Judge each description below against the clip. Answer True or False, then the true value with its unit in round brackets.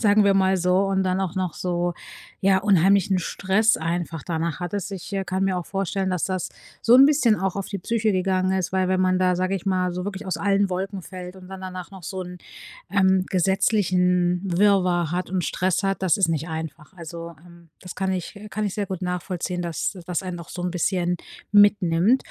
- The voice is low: False (185 Hz)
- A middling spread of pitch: False (1.7 semitones)